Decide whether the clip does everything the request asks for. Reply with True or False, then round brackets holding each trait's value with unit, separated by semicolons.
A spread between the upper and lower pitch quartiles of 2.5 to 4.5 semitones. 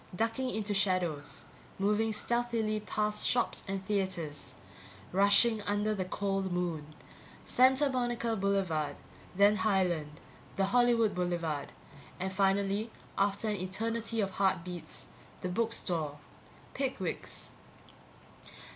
True (3.5 semitones)